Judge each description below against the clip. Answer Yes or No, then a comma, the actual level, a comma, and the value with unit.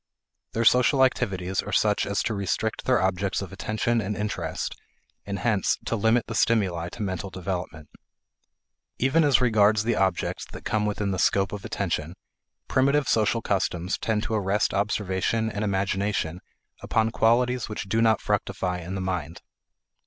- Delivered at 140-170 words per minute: Yes, average, 160 wpm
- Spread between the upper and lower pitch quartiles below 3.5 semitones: Yes, average, 3.0 semitones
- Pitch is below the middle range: Yes, low, 105 Hz